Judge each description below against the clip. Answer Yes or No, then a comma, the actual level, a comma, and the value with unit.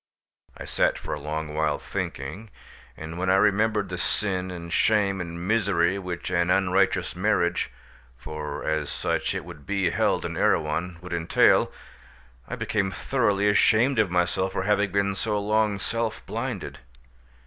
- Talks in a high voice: No, very low, 95 Hz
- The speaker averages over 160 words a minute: No, average, 150 wpm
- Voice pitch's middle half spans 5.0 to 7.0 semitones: No, average, 3.4 semitones